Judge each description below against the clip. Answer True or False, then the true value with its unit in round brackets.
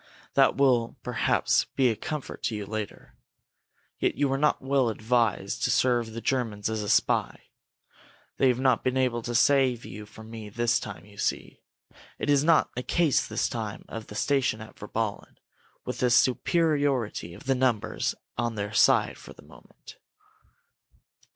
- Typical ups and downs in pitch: True (3.5 semitones)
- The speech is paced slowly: False (165 wpm)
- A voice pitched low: True (120 Hz)